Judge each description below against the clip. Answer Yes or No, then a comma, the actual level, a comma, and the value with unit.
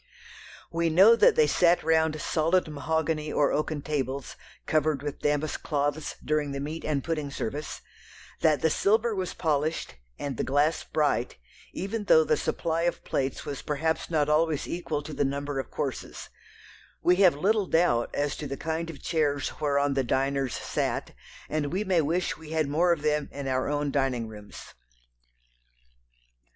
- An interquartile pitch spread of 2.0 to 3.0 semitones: Yes, narrow, 2.5 semitones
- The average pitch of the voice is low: No, medium, 150 Hz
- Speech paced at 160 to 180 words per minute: Yes, average, 165 wpm